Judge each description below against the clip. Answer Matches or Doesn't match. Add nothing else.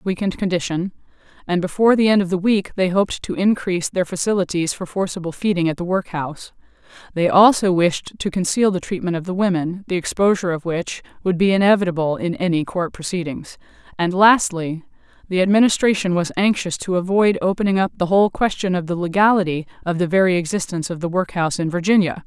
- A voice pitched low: Doesn't match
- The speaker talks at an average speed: Matches